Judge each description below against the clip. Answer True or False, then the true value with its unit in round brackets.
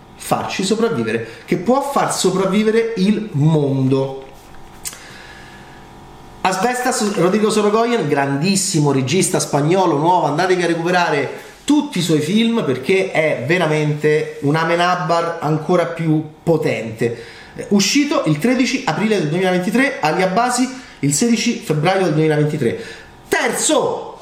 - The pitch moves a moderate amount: False (6.5 semitones)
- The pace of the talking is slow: True (105 wpm)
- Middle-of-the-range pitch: True (180 Hz)